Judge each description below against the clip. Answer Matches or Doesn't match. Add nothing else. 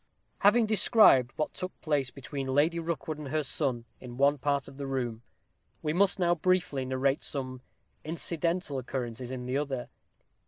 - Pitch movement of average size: Matches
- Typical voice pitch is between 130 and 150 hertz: Matches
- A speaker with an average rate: Matches